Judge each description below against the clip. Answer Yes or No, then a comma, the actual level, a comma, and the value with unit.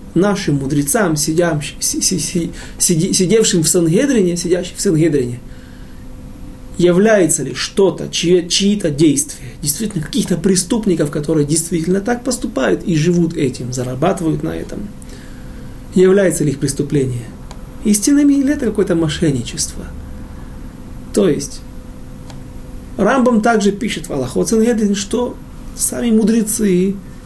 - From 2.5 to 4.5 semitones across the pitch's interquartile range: No, wide, 5.4 semitones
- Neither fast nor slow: No, slow, 100 wpm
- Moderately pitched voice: Yes, medium, 175 Hz